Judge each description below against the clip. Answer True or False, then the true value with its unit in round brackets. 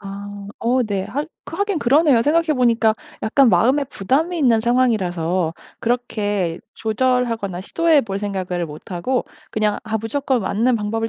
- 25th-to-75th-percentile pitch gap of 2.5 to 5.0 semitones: True (4.4 semitones)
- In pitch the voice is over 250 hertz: False (225 Hz)